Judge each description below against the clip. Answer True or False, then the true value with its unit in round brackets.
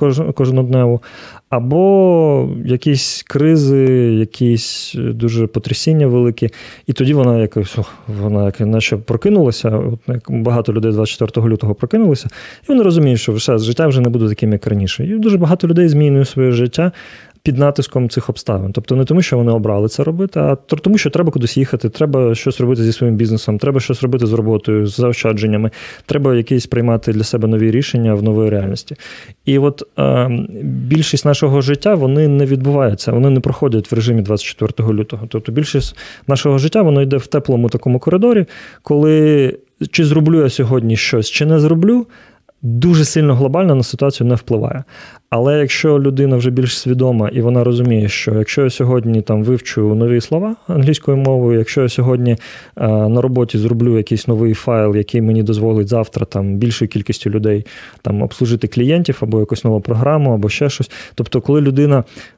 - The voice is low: True (125 Hz)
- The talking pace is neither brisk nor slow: False (170 wpm)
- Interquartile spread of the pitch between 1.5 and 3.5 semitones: False (4.1 semitones)